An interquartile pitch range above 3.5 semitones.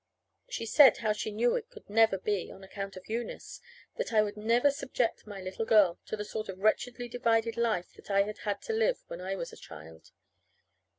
No: average, 3.2 semitones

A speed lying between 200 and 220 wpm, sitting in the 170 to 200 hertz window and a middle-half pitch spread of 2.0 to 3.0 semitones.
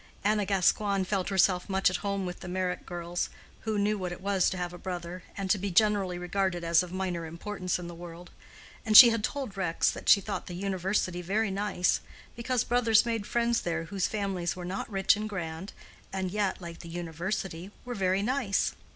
Yes: fast, 205 wpm; high, 190 Hz; average, 2.7 semitones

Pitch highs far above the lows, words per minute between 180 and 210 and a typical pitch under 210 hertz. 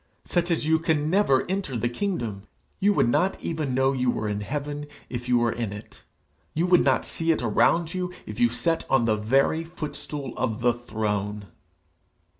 Yes: wide, 5.9 semitones; average, 190 wpm; low, 135 Hz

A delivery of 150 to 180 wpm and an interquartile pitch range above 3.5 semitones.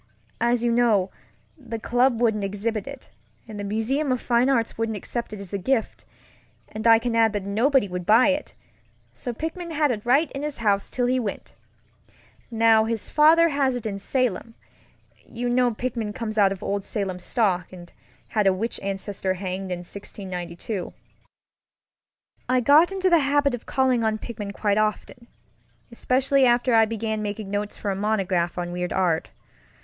Yes: average, 170 wpm; average, 4.0 semitones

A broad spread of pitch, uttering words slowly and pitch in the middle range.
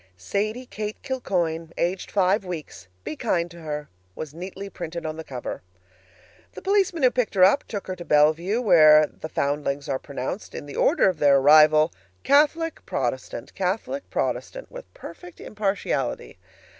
No: wide, 5.8 semitones; average, 155 wpm; medium, 175 Hz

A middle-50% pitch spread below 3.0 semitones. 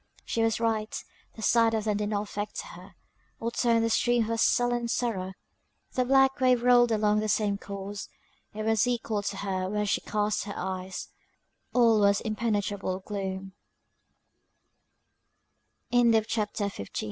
Yes: narrow, 2.4 semitones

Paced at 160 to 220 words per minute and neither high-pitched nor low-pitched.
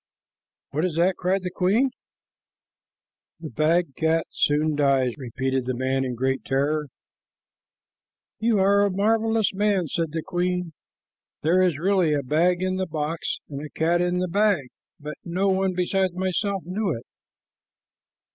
No: average, 150 wpm; medium, 175 Hz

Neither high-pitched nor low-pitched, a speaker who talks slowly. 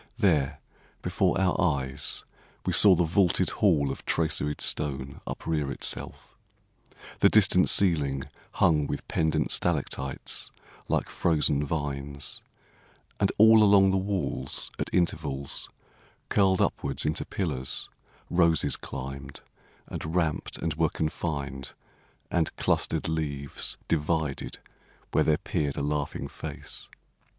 No: very low, 75 Hz; slow, 115 wpm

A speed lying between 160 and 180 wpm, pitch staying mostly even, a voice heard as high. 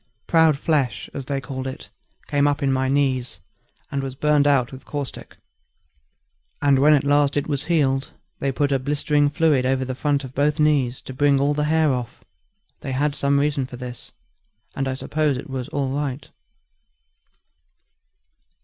No: average, 175 wpm; narrow, 1.8 semitones; medium, 140 Hz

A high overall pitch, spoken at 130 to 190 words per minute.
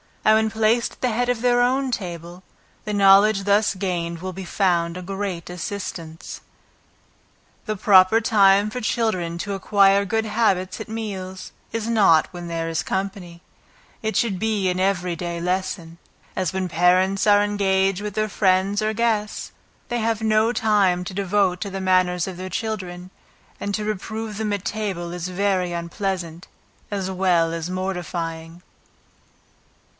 Yes: high, 195 Hz; average, 160 wpm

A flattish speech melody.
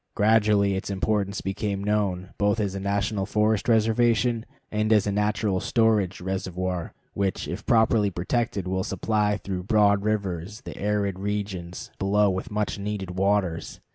Yes: narrow, 1.8 semitones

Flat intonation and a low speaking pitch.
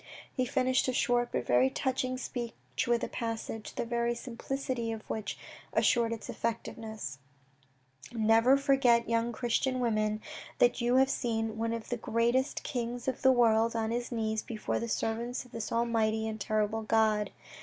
No: narrow, 1.8 semitones; high, 230 Hz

